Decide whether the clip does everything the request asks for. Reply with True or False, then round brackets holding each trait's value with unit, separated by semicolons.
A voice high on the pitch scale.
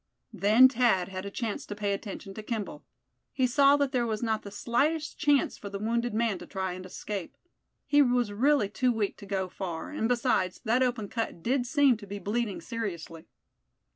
True (220 Hz)